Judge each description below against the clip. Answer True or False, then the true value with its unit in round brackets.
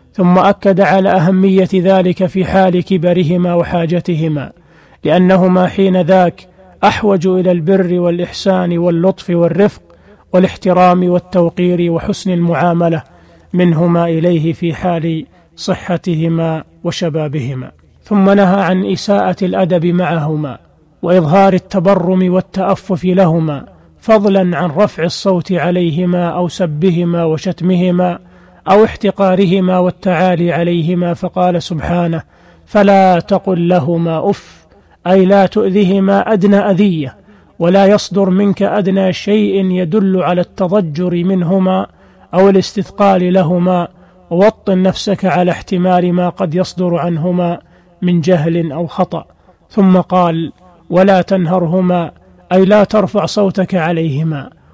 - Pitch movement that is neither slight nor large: False (1.8 semitones)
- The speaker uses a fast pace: False (105 wpm)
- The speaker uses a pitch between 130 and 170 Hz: False (180 Hz)